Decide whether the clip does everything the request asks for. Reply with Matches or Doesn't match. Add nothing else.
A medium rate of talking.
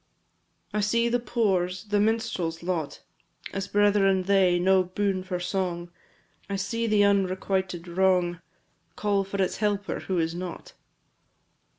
Doesn't match